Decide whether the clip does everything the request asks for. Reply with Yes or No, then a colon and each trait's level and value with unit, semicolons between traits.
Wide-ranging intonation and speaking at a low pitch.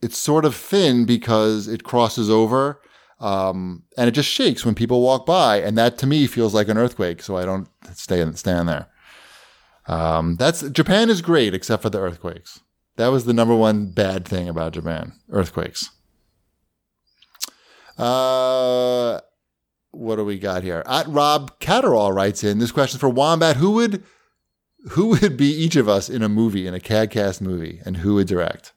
Yes: wide, 5.7 semitones; low, 115 Hz